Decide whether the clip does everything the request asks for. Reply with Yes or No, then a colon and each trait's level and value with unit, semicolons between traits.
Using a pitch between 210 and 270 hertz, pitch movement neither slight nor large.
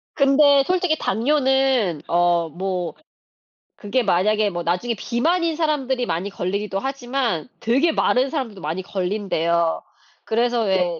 No: high, 220 Hz; wide, 7.0 semitones